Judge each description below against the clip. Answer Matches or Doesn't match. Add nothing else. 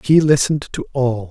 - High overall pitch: Doesn't match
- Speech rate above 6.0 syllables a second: Doesn't match